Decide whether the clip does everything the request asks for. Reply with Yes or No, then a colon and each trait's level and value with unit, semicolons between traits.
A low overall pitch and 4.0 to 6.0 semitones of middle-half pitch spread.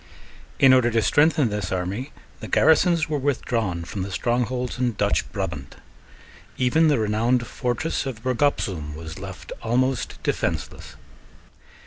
Yes: low, 120 Hz; average, 4.4 semitones